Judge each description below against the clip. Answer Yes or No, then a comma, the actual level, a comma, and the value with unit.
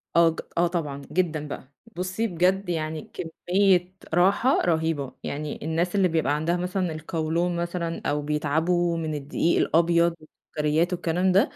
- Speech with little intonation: Yes, narrow, 2.3 semitones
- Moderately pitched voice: Yes, medium, 170 Hz